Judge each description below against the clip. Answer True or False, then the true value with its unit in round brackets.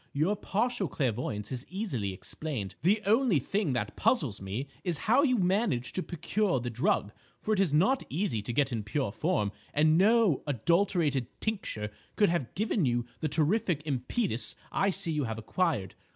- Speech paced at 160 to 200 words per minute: True (170 wpm)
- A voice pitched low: False (155 Hz)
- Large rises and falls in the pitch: True (8.6 semitones)